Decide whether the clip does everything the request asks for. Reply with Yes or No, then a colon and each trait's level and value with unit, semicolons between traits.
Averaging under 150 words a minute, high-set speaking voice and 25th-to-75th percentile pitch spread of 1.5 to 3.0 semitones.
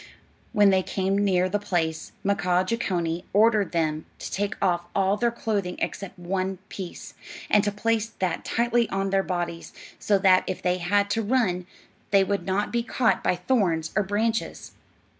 No: average, 170 wpm; high, 195 Hz; narrow, 2.6 semitones